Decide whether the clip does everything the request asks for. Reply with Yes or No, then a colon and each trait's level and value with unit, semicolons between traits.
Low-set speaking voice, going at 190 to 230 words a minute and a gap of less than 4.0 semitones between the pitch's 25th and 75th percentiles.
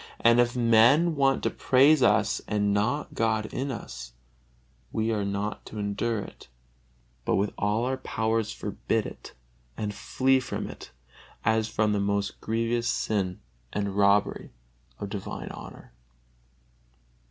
No: low, 110 Hz; average, 140 wpm; average, 2.8 semitones